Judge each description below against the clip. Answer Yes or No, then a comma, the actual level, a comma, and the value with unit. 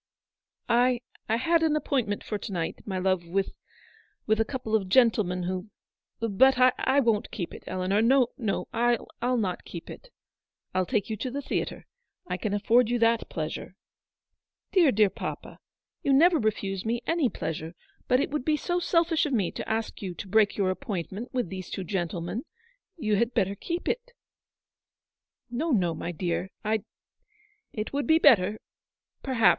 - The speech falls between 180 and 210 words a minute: Yes, average, 190 wpm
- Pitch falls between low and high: No, high, 220 Hz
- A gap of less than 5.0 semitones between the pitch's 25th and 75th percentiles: No, wide, 5.6 semitones